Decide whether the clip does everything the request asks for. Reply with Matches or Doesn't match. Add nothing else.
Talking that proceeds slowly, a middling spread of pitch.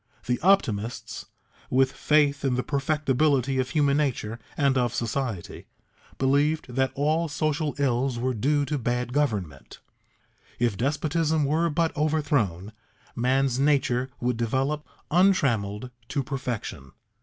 Matches